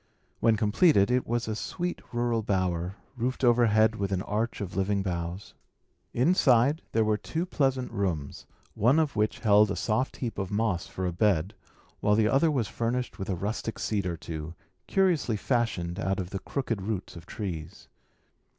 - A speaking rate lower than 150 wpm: No, average, 175 wpm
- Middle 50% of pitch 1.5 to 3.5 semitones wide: No, average, 4.0 semitones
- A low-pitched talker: Yes, low, 105 Hz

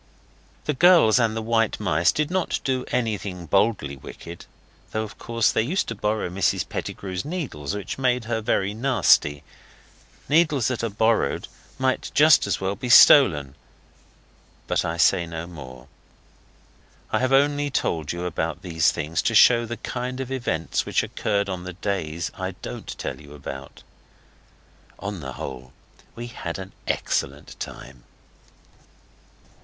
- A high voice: No, low, 105 Hz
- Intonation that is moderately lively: No, wide, 6.9 semitones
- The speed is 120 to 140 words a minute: No, average, 150 wpm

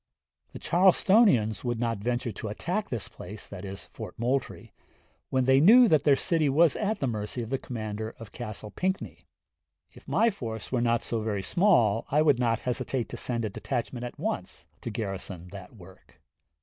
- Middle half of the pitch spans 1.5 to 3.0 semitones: No, average, 4.9 semitones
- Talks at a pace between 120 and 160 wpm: No, average, 175 wpm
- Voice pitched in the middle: No, low, 120 Hz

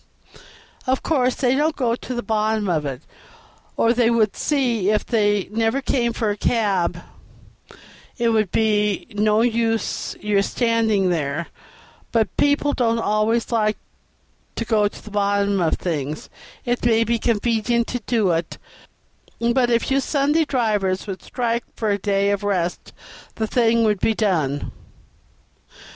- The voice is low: No, high, 220 Hz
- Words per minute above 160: No, average, 155 wpm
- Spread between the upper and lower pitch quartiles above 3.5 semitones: No, average, 2.8 semitones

